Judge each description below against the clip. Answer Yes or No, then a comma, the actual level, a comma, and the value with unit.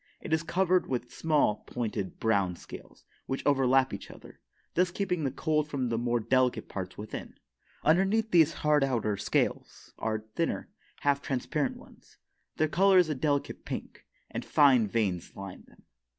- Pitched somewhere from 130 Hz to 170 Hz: Yes, low, 135 Hz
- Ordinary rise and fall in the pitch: No, wide, 5.8 semitones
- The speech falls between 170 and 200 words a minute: No, average, 160 wpm